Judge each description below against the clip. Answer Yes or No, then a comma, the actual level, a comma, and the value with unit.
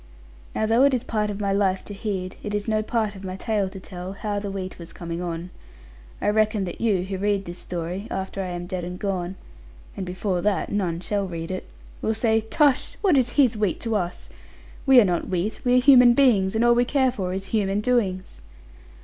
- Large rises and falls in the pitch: No, average, 3.2 semitones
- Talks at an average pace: No, fast, 225 wpm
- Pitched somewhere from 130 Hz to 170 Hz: No, high, 200 Hz